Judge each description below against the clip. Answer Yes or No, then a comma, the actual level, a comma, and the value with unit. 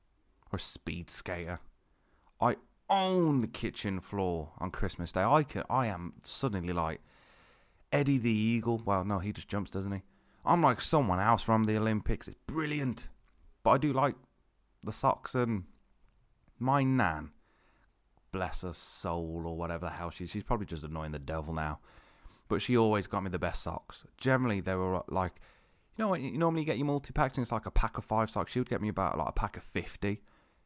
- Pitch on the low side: Yes, low, 100 Hz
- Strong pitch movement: Yes, wide, 5.7 semitones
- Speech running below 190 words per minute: No, average, 195 wpm